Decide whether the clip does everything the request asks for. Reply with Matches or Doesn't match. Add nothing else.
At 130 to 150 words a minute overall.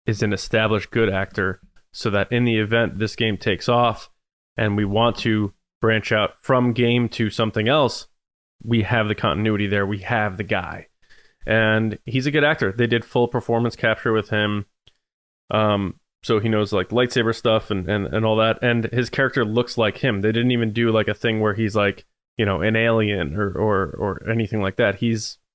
Doesn't match